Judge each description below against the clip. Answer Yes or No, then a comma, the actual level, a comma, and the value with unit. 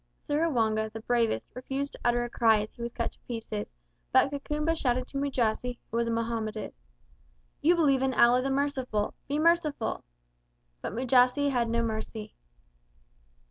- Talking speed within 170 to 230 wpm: No, average, 160 wpm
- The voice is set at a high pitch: Yes, high, 245 Hz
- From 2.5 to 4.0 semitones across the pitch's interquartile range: Yes, average, 3.5 semitones